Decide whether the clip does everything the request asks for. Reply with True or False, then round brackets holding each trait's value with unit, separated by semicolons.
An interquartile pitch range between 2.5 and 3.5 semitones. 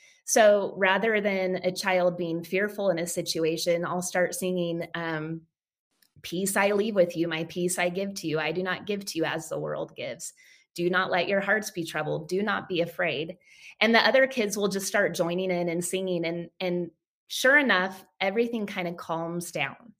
True (2.8 semitones)